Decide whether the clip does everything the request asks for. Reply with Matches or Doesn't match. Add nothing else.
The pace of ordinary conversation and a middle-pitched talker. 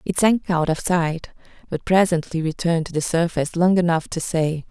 Matches